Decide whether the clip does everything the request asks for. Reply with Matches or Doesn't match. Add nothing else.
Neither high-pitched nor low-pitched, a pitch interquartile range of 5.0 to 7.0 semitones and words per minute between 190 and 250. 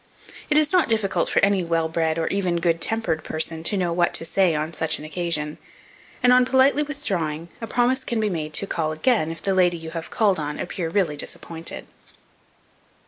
Matches